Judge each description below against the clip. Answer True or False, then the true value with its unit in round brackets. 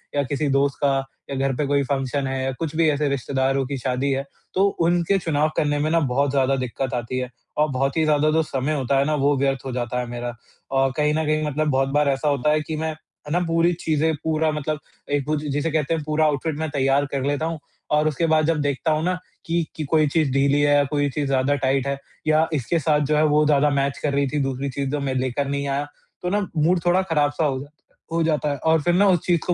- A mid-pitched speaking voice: True (145 Hz)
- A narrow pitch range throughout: True (2.3 semitones)